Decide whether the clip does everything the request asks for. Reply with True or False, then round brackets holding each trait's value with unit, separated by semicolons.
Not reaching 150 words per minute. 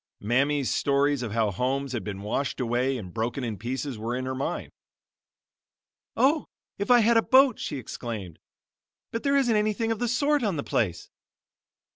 False (175 wpm)